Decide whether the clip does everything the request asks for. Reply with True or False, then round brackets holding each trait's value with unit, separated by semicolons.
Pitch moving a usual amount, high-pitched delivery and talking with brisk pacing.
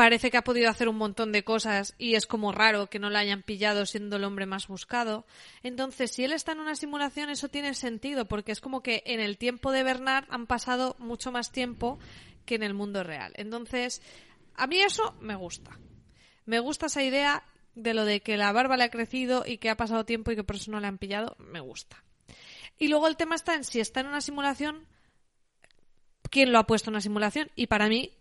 True (3.8 semitones; 235 Hz; 230 wpm)